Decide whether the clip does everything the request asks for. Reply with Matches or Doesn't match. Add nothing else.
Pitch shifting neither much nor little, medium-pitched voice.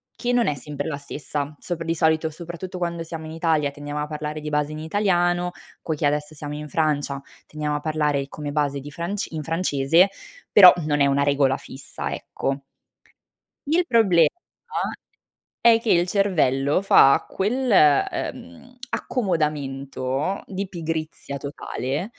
Matches